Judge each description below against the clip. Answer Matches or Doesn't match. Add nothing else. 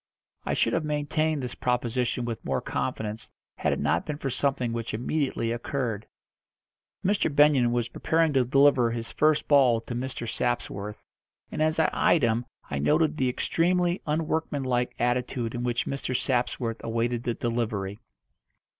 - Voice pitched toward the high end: Doesn't match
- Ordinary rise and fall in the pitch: Matches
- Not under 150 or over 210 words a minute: Matches